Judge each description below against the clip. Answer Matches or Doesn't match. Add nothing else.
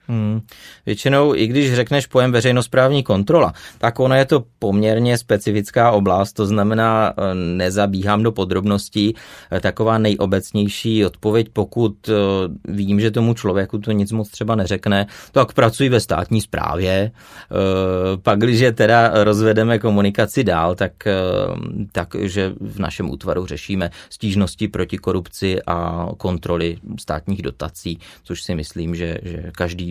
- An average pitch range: Matches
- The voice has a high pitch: Doesn't match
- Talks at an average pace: Matches